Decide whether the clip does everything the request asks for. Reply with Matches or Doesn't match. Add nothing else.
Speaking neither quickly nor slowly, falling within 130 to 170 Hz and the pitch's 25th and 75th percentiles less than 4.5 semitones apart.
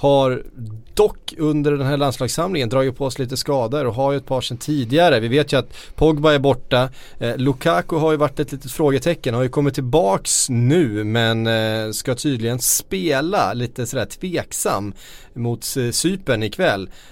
Matches